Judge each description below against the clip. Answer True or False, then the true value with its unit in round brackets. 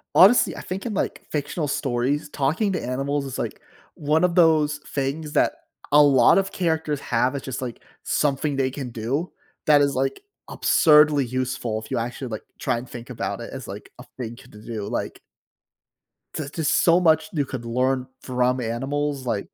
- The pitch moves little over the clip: False (3.3 semitones)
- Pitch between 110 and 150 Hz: True (140 Hz)